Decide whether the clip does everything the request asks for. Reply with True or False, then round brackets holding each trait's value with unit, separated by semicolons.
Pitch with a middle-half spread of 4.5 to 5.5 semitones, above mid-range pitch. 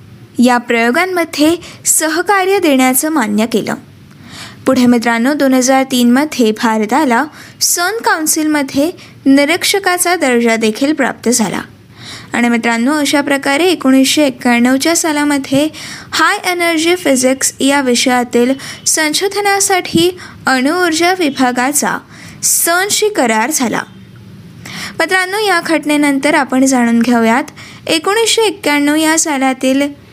True (5.1 semitones; 285 Hz)